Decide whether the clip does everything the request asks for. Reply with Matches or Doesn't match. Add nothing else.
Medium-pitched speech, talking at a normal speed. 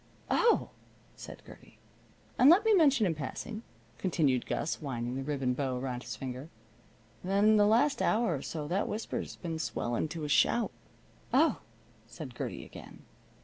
Matches